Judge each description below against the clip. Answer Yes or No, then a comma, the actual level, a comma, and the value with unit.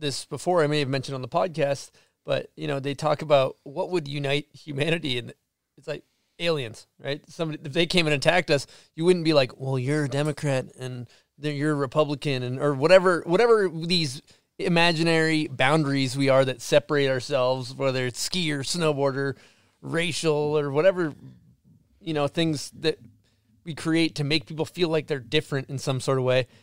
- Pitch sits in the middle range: Yes, medium, 150 Hz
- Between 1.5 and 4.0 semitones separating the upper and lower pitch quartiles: Yes, average, 2.9 semitones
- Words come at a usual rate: Yes, average, 185 wpm